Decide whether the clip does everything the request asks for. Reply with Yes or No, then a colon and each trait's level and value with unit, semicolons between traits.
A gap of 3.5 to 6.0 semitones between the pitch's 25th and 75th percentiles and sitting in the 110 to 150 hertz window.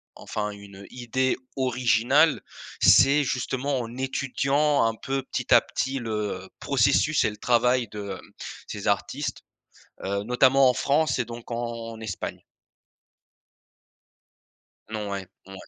Yes: average, 3.9 semitones; low, 120 Hz